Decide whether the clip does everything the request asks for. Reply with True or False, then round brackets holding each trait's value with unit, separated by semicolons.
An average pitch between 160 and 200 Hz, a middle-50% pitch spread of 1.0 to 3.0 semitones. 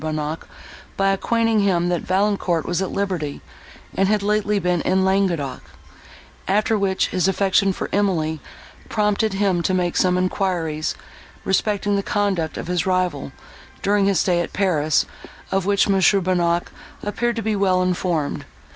True (190 Hz; 2.5 semitones)